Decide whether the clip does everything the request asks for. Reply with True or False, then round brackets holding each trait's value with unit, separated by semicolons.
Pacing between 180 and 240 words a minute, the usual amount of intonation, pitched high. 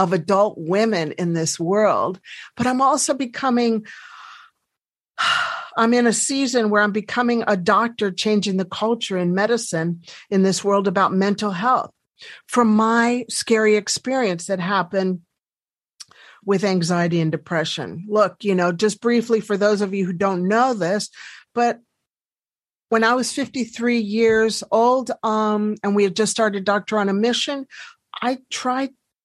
False (150 wpm; 3.5 semitones; 215 Hz)